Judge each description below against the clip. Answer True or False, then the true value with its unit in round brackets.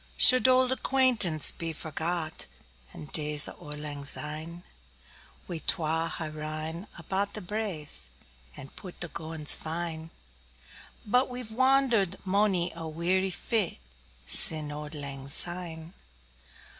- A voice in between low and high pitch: True (165 Hz)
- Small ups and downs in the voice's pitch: False (4.4 semitones)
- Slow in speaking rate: True (120 wpm)